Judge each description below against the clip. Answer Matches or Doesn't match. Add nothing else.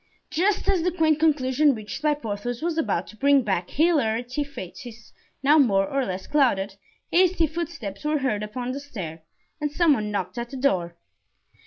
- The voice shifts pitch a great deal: Matches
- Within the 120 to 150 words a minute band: Doesn't match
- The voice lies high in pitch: Matches